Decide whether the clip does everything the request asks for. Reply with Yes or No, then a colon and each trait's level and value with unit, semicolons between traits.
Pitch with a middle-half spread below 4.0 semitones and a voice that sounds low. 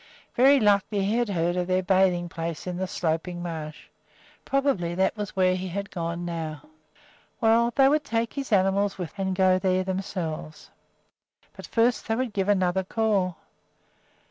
No: average, 3.3 semitones; high, 190 Hz